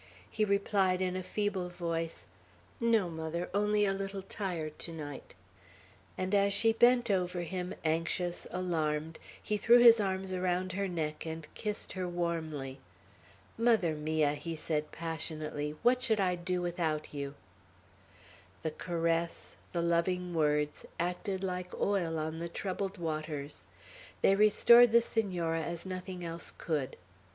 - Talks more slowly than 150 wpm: Yes, average, 140 wpm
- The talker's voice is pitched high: No, medium, 175 Hz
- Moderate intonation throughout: Yes, average, 3.3 semitones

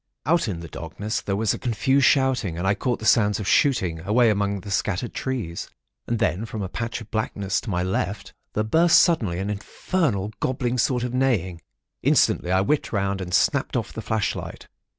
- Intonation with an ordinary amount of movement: Yes, average, 4.4 semitones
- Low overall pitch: Yes, low, 105 Hz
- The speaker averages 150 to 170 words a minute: No, average, 200 wpm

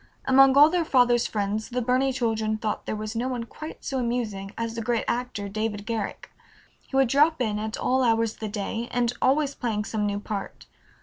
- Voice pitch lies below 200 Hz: No, high, 230 Hz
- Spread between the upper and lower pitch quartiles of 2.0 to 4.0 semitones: Yes, average, 3.0 semitones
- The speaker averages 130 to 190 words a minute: No, fast, 205 wpm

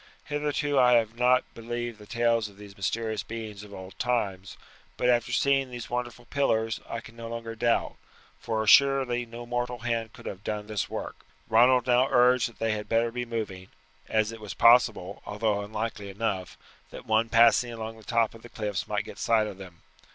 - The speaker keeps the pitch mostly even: Yes, narrow, 2.2 semitones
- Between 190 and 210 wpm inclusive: Yes, average, 195 wpm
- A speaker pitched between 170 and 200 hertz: No, low, 115 Hz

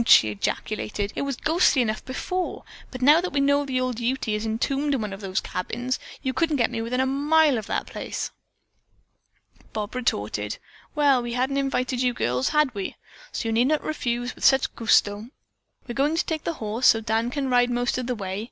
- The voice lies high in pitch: Yes, very high, 250 Hz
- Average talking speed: No, fast, 210 wpm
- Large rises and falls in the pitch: No, average, 3.9 semitones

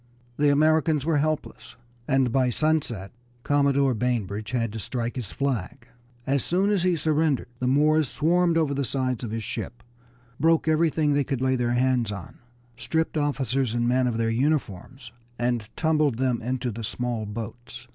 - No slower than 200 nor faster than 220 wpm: No, average, 165 wpm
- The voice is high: No, low, 130 Hz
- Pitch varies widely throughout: No, average, 4.1 semitones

